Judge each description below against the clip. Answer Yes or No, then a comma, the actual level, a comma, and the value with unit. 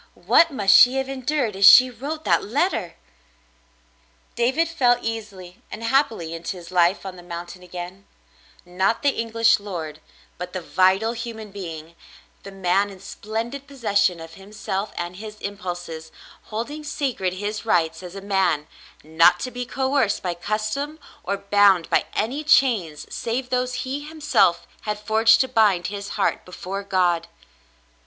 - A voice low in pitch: No, high, 205 Hz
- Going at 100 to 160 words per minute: Yes, average, 155 wpm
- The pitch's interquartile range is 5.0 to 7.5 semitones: Yes, average, 5.3 semitones